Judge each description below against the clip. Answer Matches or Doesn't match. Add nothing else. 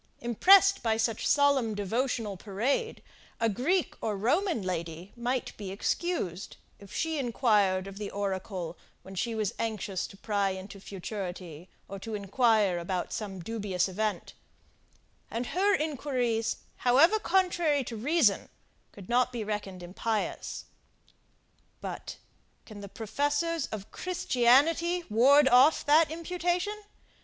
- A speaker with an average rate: Doesn't match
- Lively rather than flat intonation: Matches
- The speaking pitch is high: Matches